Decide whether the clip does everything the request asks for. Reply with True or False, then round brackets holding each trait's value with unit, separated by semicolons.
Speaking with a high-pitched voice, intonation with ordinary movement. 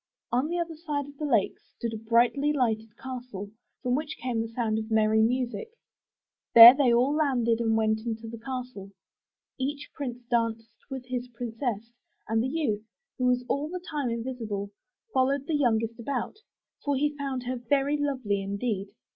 True (245 Hz; 3.7 semitones)